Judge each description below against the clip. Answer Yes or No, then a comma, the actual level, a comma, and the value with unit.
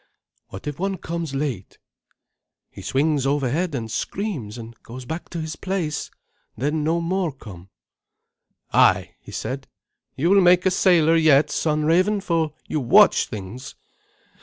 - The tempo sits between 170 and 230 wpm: No, average, 145 wpm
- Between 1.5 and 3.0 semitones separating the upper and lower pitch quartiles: No, average, 4.8 semitones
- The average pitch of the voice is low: No, medium, 155 Hz